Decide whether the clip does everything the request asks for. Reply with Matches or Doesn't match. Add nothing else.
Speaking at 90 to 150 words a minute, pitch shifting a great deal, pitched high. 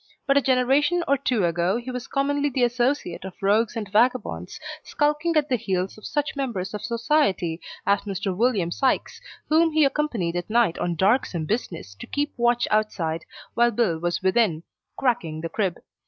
Doesn't match